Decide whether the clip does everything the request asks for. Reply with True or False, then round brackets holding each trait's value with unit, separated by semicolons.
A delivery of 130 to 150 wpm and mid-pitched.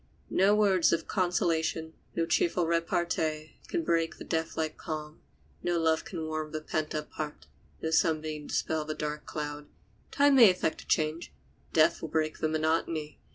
False (165 wpm; 160 Hz)